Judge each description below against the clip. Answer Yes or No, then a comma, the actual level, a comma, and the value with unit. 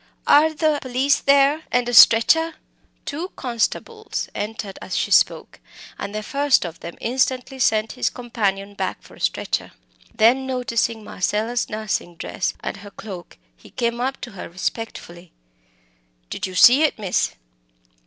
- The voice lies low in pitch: No, high, 235 Hz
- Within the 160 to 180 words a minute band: No, average, 145 wpm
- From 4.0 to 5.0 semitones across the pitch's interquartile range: Yes, average, 4.7 semitones